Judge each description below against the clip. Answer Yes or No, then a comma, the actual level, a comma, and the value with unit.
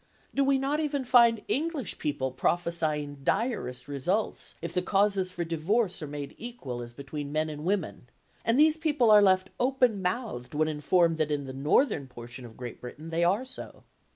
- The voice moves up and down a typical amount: No, wide, 8.4 semitones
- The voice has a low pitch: No, medium, 175 Hz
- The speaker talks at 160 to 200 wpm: Yes, average, 180 wpm